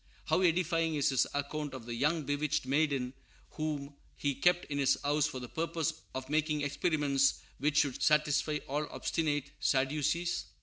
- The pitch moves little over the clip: Yes, narrow, 2.0 semitones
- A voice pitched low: No, medium, 145 Hz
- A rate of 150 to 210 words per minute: Yes, average, 160 wpm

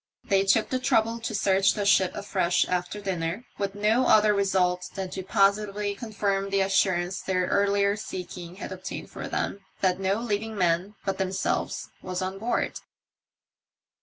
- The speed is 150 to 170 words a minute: Yes, average, 160 wpm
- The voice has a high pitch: Yes, high, 195 Hz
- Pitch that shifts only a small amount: Yes, narrow, 1.7 semitones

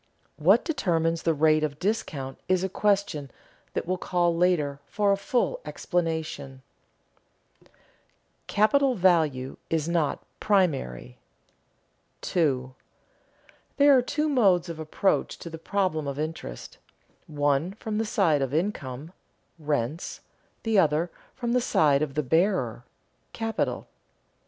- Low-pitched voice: No, medium, 165 Hz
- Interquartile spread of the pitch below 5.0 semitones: No, average, 5.3 semitones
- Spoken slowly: Yes, slow, 125 wpm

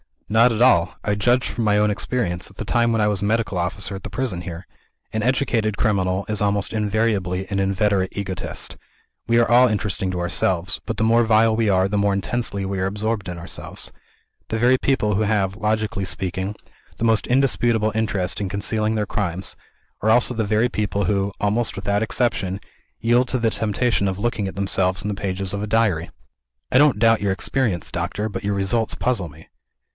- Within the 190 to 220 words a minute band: Yes, average, 200 wpm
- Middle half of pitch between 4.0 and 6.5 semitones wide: No, average, 2.7 semitones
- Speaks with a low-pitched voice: Yes, low, 105 Hz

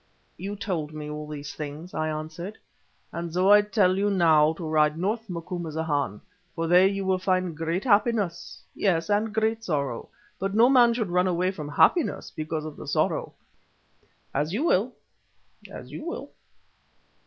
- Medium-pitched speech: Yes, medium, 180 Hz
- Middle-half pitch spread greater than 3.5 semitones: Yes, average, 4.6 semitones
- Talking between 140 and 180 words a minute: Yes, average, 160 wpm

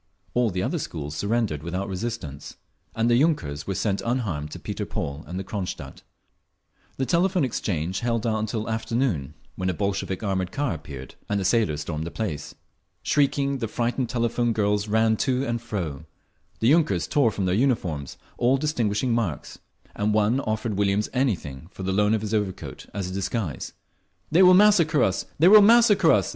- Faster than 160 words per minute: Yes, average, 175 wpm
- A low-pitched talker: Yes, low, 110 Hz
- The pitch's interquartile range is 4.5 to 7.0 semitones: Yes, average, 4.9 semitones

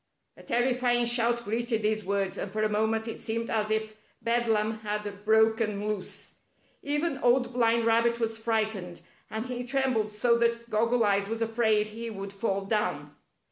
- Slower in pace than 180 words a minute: Yes, average, 165 wpm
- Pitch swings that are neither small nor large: No, narrow, 1.8 semitones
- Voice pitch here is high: Yes, high, 225 Hz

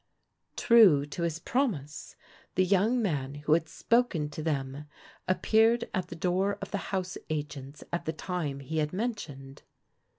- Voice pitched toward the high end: No, medium, 165 Hz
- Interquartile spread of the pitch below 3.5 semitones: No, average, 5.3 semitones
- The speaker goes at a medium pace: Yes, average, 155 wpm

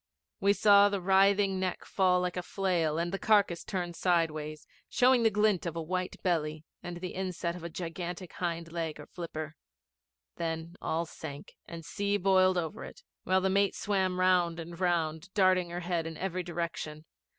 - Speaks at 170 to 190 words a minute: Yes, average, 175 wpm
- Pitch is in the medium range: Yes, medium, 180 Hz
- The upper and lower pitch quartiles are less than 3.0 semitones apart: Yes, narrow, 2.4 semitones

